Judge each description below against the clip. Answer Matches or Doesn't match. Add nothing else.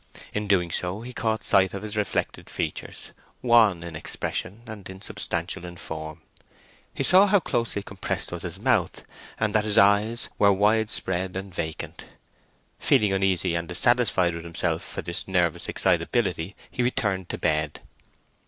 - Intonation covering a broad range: Doesn't match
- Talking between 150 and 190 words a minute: Matches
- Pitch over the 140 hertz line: Doesn't match